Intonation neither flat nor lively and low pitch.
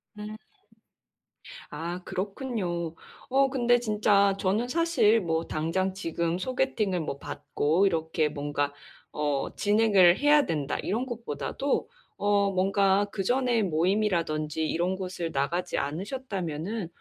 No: average, 5.0 semitones; high, 190 Hz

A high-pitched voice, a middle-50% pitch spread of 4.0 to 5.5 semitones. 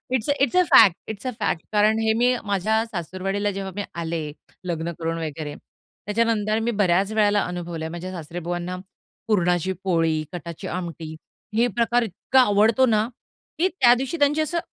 Yes: high, 195 Hz; average, 4.7 semitones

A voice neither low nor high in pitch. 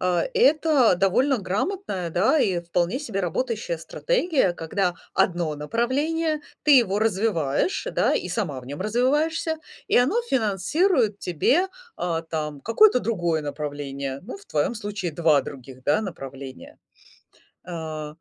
No: high, 195 Hz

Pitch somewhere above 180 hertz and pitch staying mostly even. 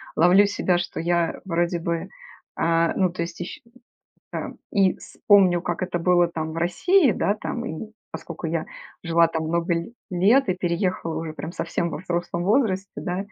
No: medium, 175 Hz; narrow, 2.1 semitones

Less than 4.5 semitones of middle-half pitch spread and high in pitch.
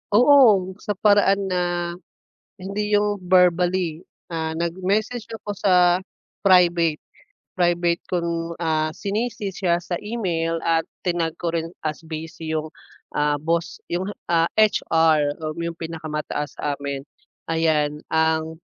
No: average, 2.8 semitones; medium, 170 Hz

